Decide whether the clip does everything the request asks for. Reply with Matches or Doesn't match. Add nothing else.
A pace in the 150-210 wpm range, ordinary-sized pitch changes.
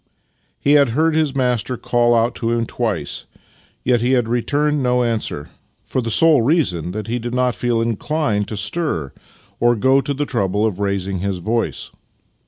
Matches